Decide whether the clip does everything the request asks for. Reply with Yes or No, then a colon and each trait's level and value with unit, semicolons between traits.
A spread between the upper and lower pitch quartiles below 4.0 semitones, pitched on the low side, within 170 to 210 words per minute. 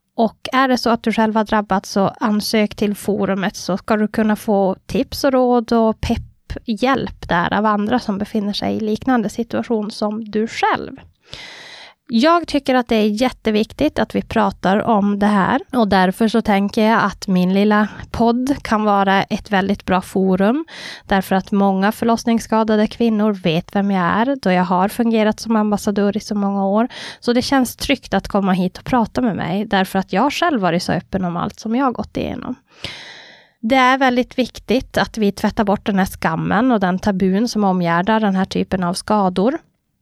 No: average, 3.2 semitones; high, 215 Hz; average, 190 wpm